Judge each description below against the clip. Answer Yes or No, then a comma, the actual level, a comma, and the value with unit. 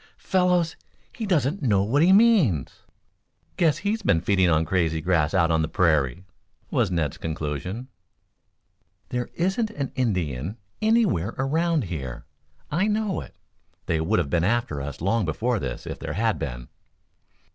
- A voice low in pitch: Yes, low, 100 Hz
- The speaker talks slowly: No, average, 150 wpm